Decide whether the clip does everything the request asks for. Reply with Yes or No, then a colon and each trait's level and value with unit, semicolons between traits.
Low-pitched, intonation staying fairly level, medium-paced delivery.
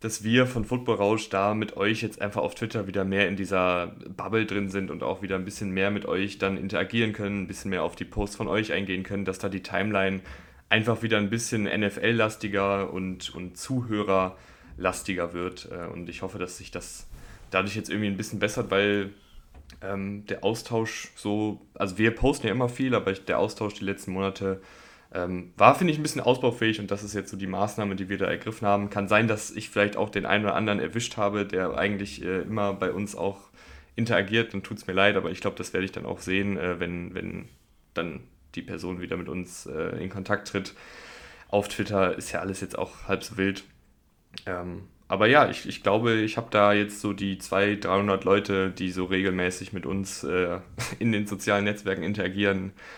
No: low, 100 Hz; narrow, 1.9 semitones; fast, 210 wpm